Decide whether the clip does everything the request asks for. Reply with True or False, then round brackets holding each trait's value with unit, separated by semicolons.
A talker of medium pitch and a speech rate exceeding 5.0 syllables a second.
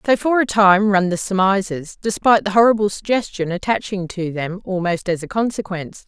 False (195 Hz; 5.4 syllables/s)